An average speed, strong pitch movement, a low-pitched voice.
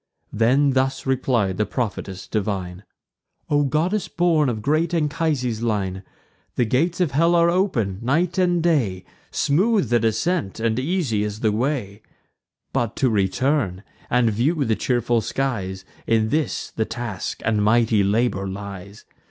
Yes: average, 145 wpm; wide, 6.4 semitones; low, 120 Hz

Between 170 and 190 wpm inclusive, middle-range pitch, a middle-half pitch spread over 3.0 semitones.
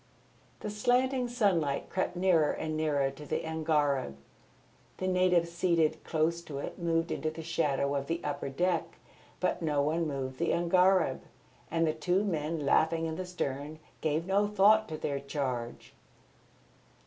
No: average, 155 wpm; medium, 165 Hz; average, 3.6 semitones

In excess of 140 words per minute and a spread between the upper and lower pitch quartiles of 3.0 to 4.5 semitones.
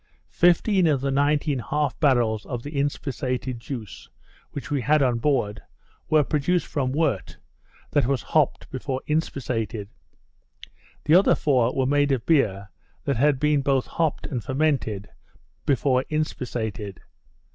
No: slow, 135 wpm; average, 3.5 semitones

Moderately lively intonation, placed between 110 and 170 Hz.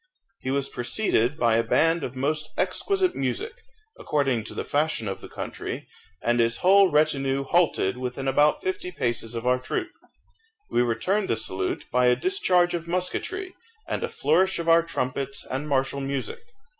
No: wide, 5.9 semitones; medium, 140 Hz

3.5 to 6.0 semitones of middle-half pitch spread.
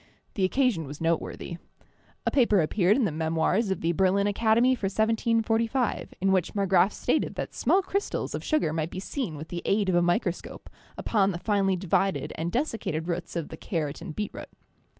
Yes: average, 4.5 semitones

